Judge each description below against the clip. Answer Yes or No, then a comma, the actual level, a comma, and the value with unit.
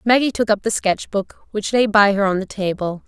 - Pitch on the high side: Yes, high, 205 Hz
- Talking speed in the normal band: No, fast, 255 wpm